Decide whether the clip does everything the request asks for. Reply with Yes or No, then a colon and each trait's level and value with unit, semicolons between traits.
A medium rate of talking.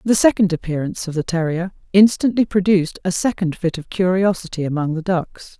Yes: average, 170 wpm